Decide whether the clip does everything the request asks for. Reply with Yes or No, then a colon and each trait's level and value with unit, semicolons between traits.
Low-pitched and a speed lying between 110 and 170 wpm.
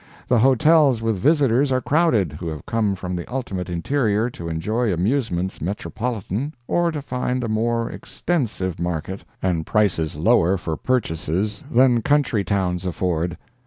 Yes: low, 105 Hz; average, 145 wpm